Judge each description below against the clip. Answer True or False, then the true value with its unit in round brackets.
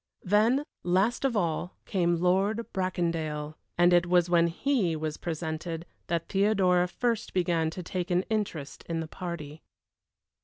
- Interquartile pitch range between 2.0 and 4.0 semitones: True (2.7 semitones)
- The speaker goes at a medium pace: True (145 wpm)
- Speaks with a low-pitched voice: False (175 Hz)